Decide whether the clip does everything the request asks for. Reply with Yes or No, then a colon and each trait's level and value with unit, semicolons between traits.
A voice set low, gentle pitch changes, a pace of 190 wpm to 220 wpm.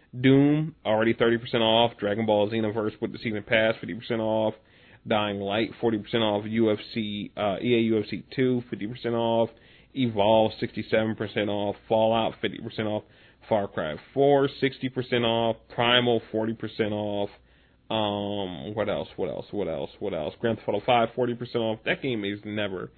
No: low, 110 Hz; narrow, 2.0 semitones; average, 150 wpm